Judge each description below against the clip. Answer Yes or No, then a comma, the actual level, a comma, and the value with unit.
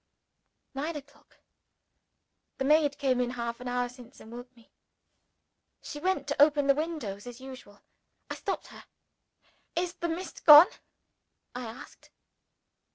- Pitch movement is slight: No, average, 3.5 semitones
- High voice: Yes, very high, 270 Hz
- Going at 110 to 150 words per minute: Yes, average, 140 wpm